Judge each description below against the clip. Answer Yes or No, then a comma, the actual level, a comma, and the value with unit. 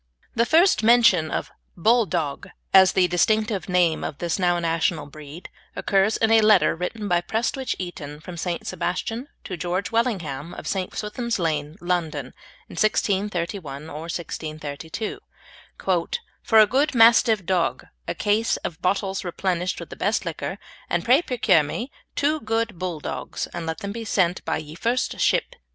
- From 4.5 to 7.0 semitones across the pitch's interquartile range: Yes, average, 5.0 semitones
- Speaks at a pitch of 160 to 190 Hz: Yes, medium, 185 Hz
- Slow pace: No, average, 155 wpm